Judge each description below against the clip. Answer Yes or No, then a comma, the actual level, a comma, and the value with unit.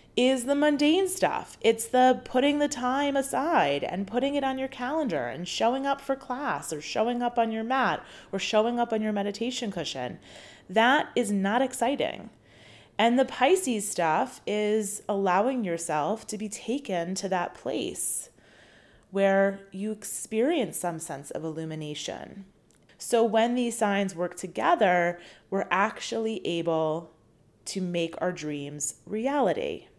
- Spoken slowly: No, average, 145 wpm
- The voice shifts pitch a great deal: Yes, wide, 5.9 semitones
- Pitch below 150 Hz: No, high, 215 Hz